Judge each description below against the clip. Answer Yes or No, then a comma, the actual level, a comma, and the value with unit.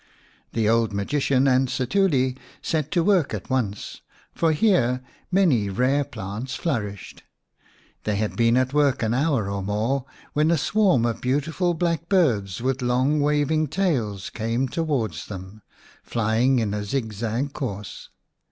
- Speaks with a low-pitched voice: Yes, low, 130 Hz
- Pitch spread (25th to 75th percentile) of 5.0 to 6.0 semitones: Yes, average, 5.3 semitones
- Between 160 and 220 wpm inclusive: No, average, 145 wpm